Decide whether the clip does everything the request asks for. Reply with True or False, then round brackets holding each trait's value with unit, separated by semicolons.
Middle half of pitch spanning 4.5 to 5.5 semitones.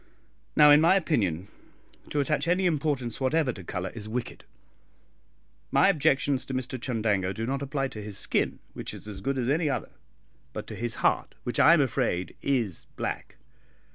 True (5.2 semitones)